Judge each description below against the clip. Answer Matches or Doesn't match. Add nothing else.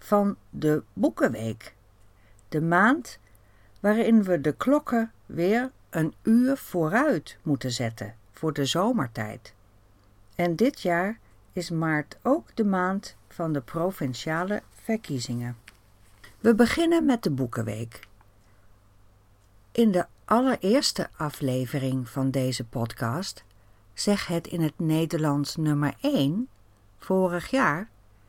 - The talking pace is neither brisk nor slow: Doesn't match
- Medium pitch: Matches